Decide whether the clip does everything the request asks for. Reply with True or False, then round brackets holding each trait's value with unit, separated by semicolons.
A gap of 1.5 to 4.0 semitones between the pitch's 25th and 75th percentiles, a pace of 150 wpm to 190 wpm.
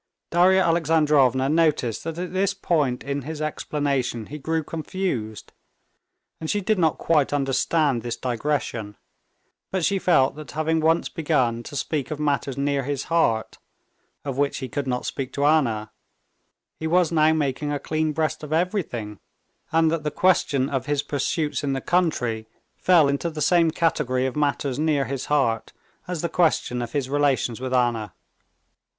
True (3.6 semitones; 165 wpm)